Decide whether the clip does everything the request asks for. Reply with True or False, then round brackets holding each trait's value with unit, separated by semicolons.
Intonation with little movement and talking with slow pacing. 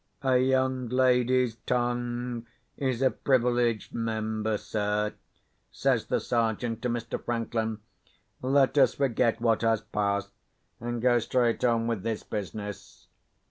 True (2.2 semitones; 125 wpm)